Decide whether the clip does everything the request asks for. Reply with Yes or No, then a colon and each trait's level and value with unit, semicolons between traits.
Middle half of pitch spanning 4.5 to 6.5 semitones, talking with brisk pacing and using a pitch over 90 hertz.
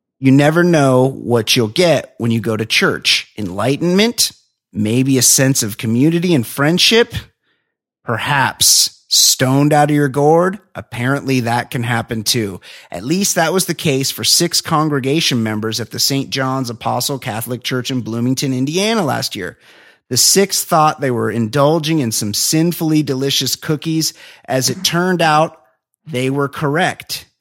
No: average, 4.8 semitones; average, 155 wpm; low, 135 Hz